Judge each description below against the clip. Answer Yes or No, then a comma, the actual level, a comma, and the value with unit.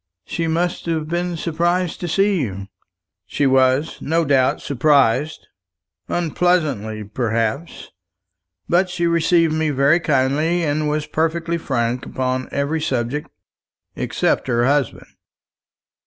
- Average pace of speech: No, slow, 115 wpm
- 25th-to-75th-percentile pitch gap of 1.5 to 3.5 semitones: No, average, 4.4 semitones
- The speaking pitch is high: No, medium, 150 Hz